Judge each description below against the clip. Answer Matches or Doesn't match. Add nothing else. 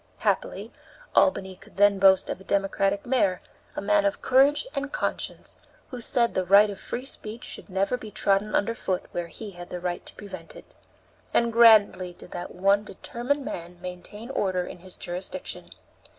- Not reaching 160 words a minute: Doesn't match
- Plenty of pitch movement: Doesn't match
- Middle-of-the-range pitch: Doesn't match